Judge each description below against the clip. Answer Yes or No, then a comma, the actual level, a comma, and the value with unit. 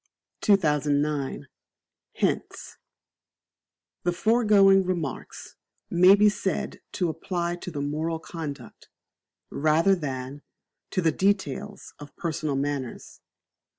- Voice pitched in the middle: Yes, medium, 165 Hz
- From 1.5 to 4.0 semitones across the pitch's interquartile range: No, average, 4.7 semitones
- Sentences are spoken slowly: Yes, slow, 95 wpm